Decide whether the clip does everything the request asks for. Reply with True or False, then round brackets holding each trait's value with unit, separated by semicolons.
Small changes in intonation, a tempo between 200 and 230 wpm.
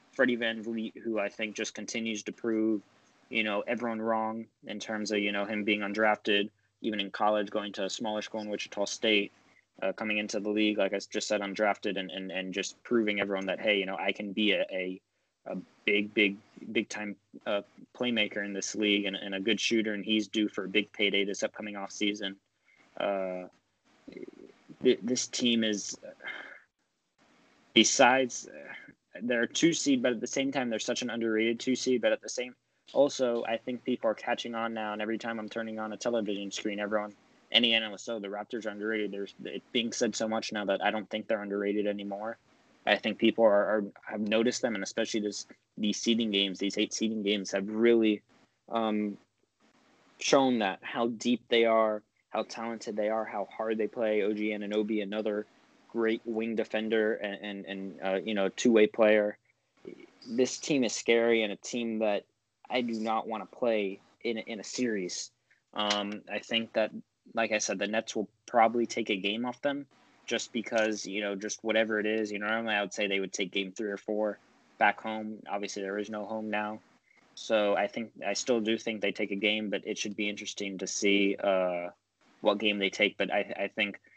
True (1.8 semitones; 205 wpm)